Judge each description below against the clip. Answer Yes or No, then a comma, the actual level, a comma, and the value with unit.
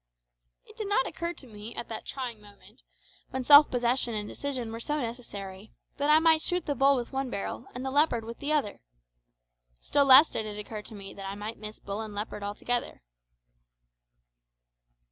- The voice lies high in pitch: Yes, high, 240 Hz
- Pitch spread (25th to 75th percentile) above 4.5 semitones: Yes, average, 5.1 semitones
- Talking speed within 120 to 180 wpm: No, average, 190 wpm